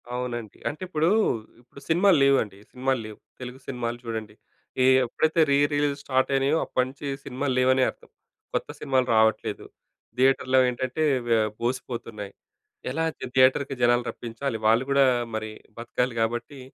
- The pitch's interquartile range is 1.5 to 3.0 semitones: Yes, average, 2.7 semitones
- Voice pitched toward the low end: Yes, low, 130 Hz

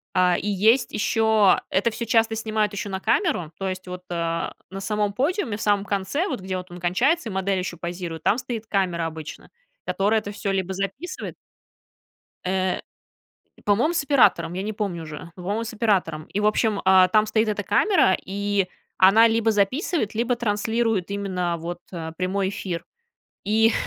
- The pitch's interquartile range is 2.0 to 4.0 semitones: Yes, average, 3.3 semitones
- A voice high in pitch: Yes, high, 200 Hz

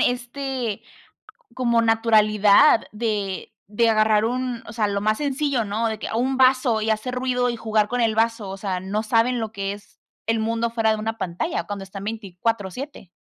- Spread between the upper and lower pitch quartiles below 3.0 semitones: Yes, narrow, 2.6 semitones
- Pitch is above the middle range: Yes, high, 225 Hz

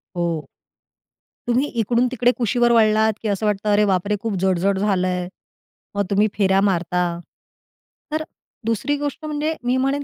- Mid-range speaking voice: No, high, 215 Hz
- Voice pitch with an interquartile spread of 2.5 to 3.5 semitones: No, average, 4.1 semitones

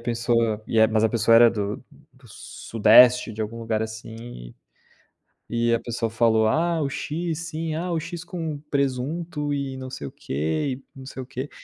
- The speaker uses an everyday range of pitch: Yes, average, 4.8 semitones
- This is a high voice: No, low, 120 Hz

